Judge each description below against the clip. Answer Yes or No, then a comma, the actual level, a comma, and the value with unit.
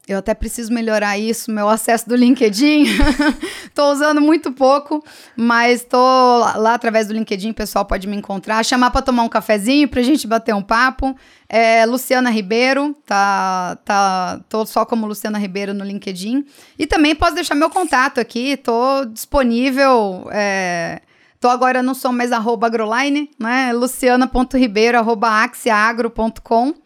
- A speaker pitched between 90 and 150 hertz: No, high, 240 Hz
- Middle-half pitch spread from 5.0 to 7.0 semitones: No, average, 3.4 semitones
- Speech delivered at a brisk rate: No, average, 145 wpm